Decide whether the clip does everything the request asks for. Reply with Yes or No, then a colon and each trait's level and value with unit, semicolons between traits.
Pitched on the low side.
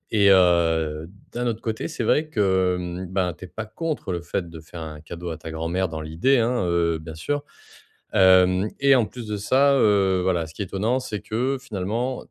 Yes: very low, 95 Hz